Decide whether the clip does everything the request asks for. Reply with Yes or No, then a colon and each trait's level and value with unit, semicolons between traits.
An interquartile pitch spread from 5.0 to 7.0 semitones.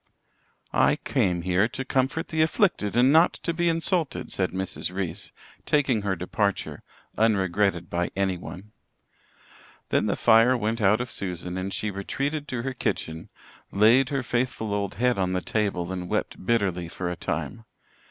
Yes: wide, 5.4 semitones